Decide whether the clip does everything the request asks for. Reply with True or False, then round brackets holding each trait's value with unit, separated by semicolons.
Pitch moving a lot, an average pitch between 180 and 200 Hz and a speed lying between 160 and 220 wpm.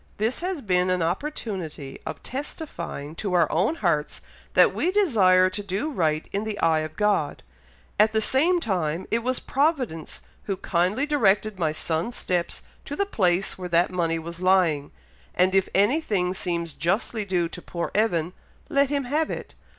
True (6.1 semitones; 190 Hz; 170 wpm)